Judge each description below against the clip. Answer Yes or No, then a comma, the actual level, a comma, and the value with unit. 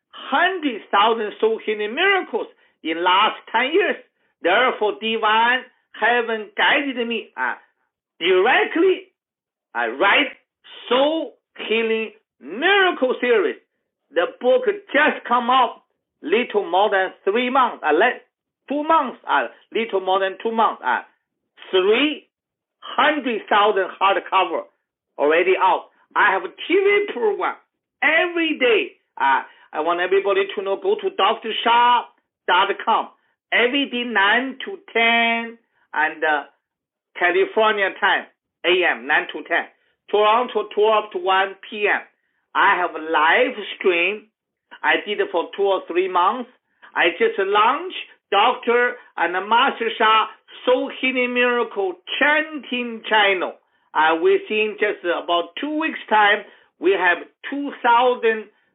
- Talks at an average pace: No, slow, 125 wpm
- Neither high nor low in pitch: No, high, 245 Hz